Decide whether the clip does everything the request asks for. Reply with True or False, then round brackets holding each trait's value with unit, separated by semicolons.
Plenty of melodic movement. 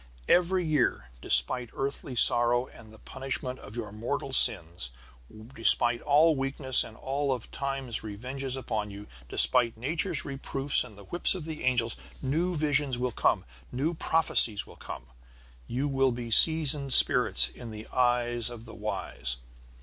False (3.5 semitones)